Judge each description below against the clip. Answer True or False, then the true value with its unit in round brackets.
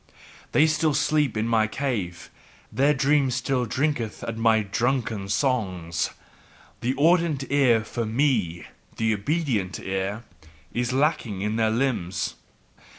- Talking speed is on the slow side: True (130 wpm)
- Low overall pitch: True (120 Hz)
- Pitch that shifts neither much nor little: True (4.7 semitones)